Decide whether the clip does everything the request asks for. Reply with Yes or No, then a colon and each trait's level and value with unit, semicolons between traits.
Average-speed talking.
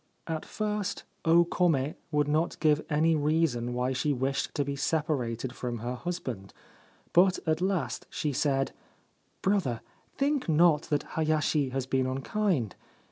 Yes: average, 145 wpm